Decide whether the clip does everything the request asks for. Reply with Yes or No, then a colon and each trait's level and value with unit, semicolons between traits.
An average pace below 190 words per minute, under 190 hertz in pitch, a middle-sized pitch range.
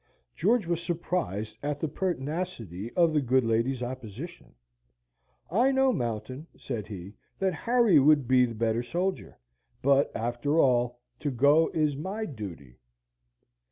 No: slow, 135 wpm; medium, 140 Hz; wide, 6.6 semitones